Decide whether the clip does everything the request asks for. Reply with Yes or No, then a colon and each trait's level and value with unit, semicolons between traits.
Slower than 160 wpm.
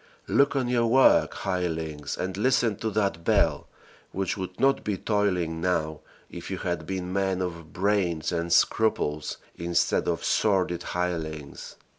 Yes: average, 145 wpm